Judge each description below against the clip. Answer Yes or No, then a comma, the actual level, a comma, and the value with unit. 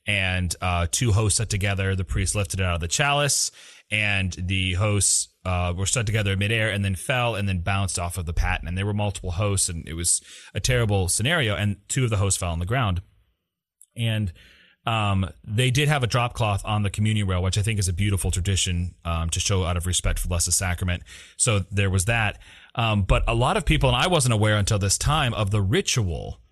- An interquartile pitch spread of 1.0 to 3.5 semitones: Yes, average, 3.1 semitones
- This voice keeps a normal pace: No, fast, 230 wpm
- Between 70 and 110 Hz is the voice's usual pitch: Yes, low, 100 Hz